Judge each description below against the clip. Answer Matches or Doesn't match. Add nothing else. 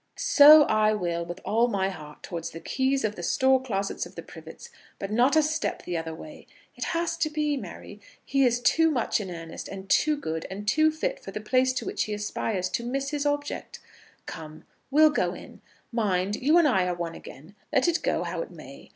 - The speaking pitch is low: Doesn't match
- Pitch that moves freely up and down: Matches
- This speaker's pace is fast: Matches